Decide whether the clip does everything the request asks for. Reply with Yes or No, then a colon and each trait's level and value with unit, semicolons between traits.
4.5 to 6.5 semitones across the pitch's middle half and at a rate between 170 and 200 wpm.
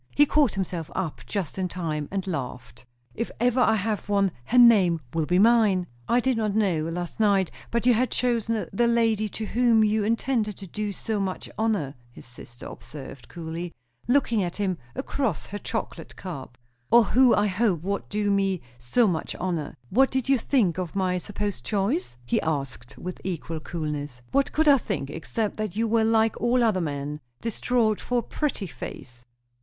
Yes: average, 5.3 semitones; average, 185 wpm